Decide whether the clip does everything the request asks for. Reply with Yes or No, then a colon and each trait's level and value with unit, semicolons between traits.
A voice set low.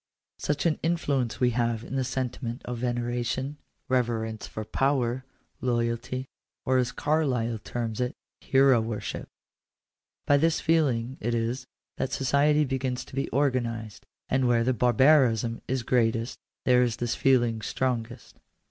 Yes: low, 125 Hz